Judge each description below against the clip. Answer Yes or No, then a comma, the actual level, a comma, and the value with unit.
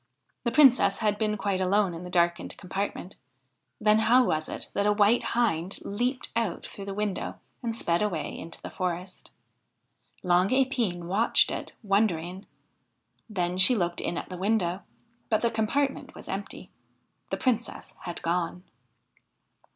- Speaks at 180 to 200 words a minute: No, average, 150 wpm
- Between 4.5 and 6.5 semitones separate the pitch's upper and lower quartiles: No, average, 4.0 semitones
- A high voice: Yes, high, 200 Hz